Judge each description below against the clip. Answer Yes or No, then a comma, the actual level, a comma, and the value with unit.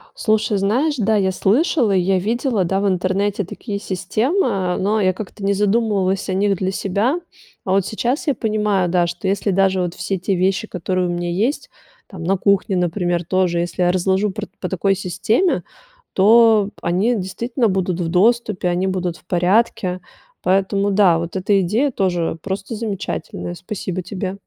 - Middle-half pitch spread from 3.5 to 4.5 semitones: No, average, 2.7 semitones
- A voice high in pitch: Yes, high, 195 Hz